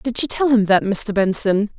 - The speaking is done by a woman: Yes, female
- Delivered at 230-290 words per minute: Yes, fast, 235 wpm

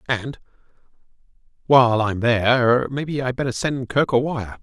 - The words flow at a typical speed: Yes, average, 145 wpm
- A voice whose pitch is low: Yes, low, 125 Hz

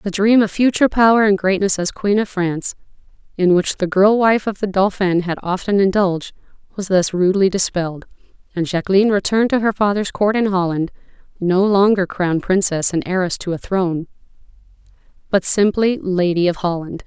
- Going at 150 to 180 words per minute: Yes, average, 170 wpm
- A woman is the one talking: Yes, female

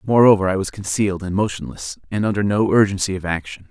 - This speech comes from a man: Yes, male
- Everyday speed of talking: Yes, average, 195 wpm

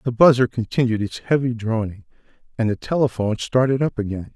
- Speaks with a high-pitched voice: No, low, 120 Hz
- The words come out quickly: No, average, 165 wpm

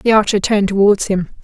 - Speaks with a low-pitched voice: No, high, 200 Hz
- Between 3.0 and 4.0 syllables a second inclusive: No, 6.6 syllables/s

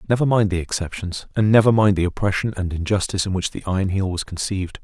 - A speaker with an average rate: No, fast, 225 wpm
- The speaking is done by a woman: No, male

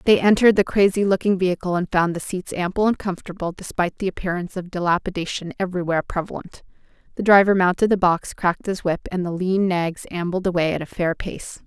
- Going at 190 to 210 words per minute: Yes, average, 195 wpm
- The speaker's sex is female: Yes, female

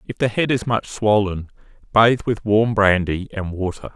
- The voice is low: Yes, low, 105 Hz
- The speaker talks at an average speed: Yes, average, 180 wpm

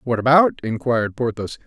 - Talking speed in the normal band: Yes, average, 145 wpm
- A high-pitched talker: No, low, 120 Hz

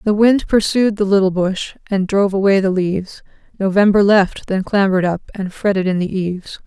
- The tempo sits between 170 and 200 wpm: Yes, average, 190 wpm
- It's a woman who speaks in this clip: Yes, female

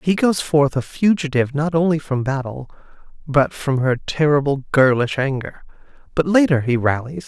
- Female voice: No, male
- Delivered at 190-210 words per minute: No, average, 155 wpm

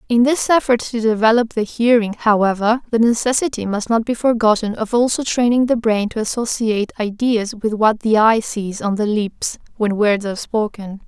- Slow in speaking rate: No, average, 185 wpm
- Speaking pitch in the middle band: No, high, 220 Hz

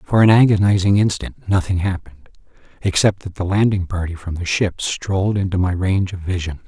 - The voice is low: Yes, very low, 95 Hz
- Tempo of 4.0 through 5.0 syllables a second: No, 5.6 syllables/s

